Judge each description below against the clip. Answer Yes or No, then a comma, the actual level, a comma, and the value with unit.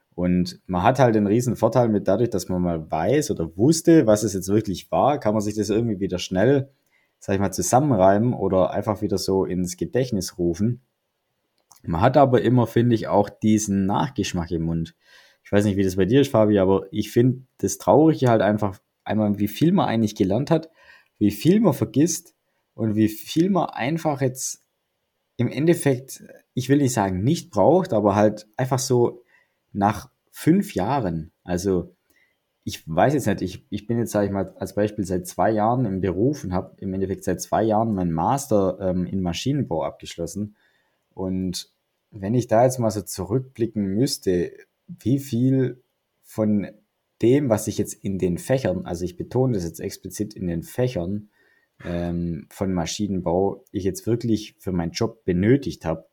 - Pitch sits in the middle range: No, low, 105 Hz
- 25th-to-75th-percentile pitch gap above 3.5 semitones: Yes, average, 5.1 semitones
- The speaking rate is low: No, average, 180 wpm